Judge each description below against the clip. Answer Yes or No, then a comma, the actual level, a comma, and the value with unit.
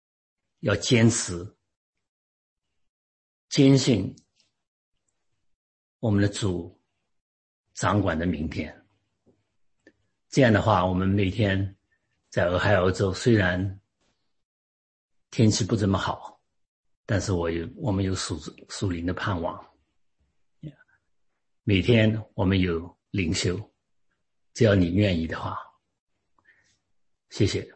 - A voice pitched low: Yes, very low, 95 Hz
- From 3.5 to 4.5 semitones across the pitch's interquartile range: Yes, average, 3.8 semitones